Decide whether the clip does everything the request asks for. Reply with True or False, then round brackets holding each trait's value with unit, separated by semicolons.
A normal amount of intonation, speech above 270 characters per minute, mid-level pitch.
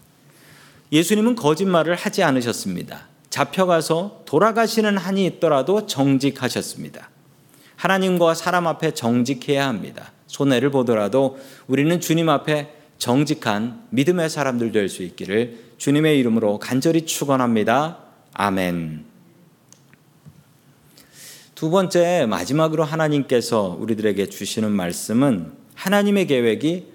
True (4.2 semitones; 285 characters per minute; 150 Hz)